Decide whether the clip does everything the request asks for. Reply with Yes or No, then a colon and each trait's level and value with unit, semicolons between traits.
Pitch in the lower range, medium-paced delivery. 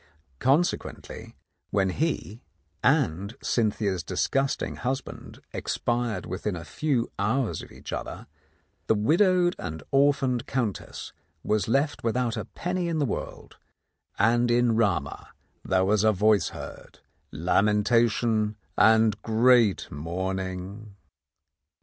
No: low, 110 Hz; slow, 115 wpm